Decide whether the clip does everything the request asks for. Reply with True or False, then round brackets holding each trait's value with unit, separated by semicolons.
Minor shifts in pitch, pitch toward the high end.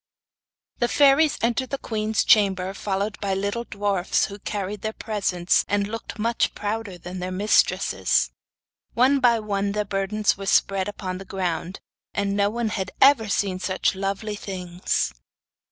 True (2.3 semitones; 200 Hz)